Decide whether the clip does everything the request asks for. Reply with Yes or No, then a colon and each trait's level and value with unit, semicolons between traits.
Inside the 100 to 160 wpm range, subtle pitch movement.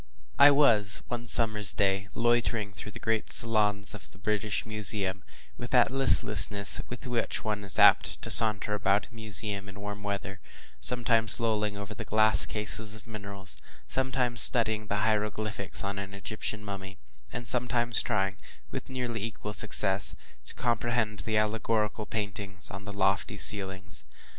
Yes: average, 155 wpm; narrow, 2.2 semitones